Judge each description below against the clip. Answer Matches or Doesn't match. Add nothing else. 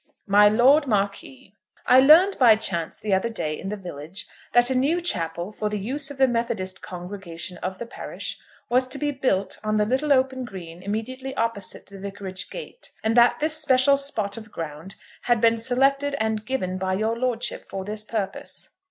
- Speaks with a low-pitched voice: Doesn't match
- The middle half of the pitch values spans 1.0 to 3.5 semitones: Doesn't match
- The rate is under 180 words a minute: Doesn't match